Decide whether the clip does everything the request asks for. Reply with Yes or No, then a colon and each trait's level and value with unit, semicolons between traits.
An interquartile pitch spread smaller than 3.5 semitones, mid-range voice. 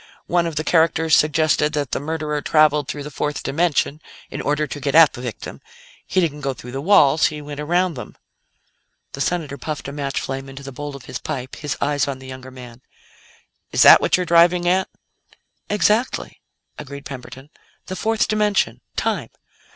Yes: average, 3.1 semitones; medium, 150 Hz